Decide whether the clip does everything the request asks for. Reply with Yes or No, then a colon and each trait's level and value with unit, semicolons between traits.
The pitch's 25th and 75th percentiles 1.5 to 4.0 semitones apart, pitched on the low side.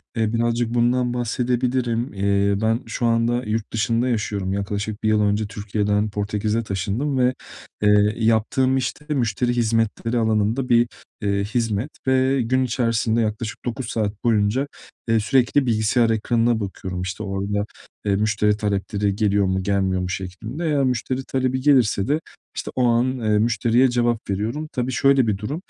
Yes: average, 3.0 semitones; low, 115 Hz